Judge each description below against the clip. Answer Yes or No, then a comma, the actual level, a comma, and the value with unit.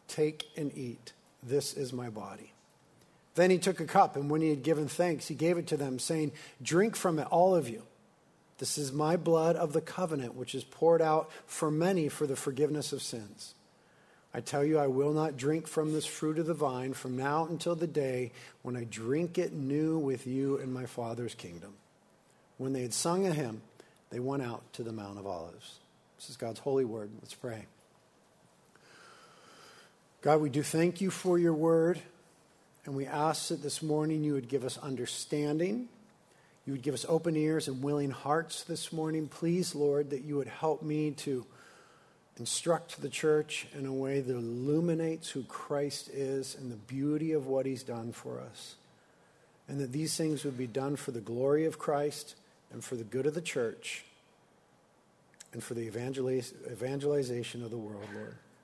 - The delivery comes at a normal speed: Yes, average, 190 wpm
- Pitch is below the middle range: No, medium, 145 Hz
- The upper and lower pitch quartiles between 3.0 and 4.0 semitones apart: Yes, average, 3.6 semitones